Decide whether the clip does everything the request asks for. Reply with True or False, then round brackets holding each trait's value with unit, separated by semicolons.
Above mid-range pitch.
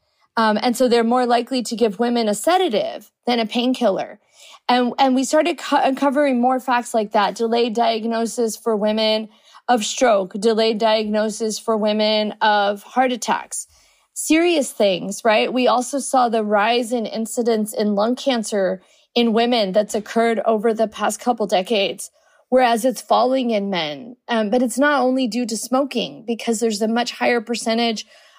True (235 Hz)